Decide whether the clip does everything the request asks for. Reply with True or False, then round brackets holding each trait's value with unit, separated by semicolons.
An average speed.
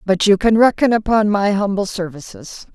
True (175 wpm)